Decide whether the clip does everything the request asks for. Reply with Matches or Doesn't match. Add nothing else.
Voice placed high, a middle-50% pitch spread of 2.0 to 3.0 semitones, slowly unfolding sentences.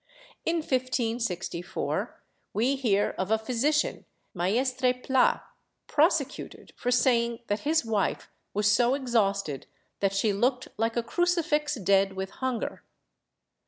Doesn't match